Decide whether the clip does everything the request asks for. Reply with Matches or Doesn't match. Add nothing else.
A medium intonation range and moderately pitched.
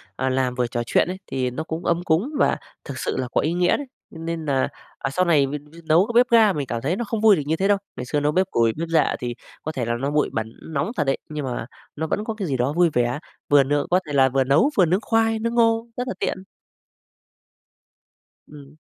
Doesn't match